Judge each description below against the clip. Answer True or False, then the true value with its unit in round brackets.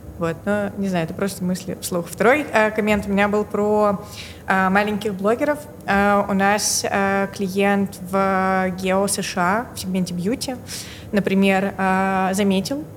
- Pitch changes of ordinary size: False (1.5 semitones)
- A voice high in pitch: True (200 Hz)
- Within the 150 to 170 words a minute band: True (155 wpm)